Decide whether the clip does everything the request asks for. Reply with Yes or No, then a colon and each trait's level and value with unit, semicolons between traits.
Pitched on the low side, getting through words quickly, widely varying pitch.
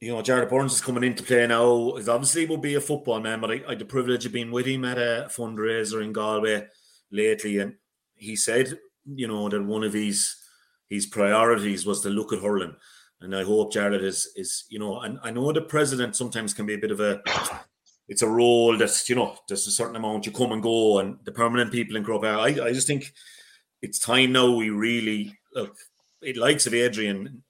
No: low, 115 Hz; fast, 225 wpm; average, 2.7 semitones